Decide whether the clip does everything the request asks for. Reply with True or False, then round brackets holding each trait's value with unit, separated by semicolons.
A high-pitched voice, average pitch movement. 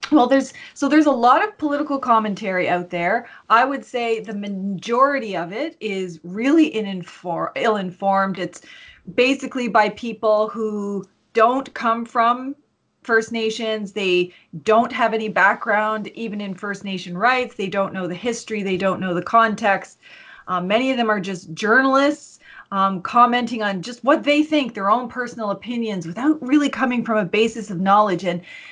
True (220 Hz; 4.4 semitones)